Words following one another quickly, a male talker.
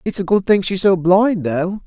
Yes: fast, 260 wpm; male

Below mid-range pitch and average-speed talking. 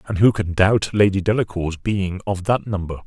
Yes: low, 100 Hz; average, 195 wpm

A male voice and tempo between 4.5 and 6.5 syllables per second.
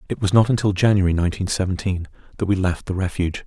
No: male; 7.1 syllables/s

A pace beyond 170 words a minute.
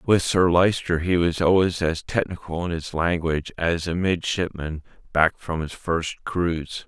No: average, 165 wpm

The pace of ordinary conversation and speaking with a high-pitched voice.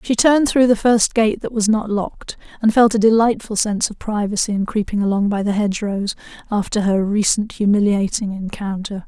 Yes: average, 185 wpm; high, 210 Hz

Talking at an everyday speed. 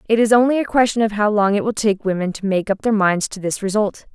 No: fast, 290 wpm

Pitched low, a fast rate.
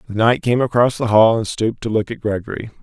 Yes: low, 110 Hz; fast, 255 wpm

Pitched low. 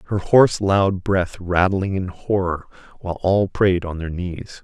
Yes: very low, 95 Hz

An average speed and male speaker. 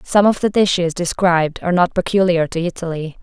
No: average, 185 wpm; female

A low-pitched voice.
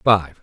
Yes: very low, 90 Hz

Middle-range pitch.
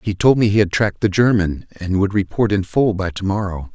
No: low, 100 Hz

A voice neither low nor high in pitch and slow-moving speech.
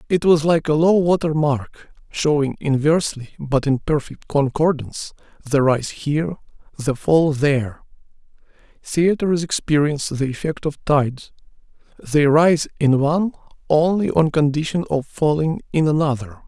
Yes: medium, 150 Hz; slow, 130 wpm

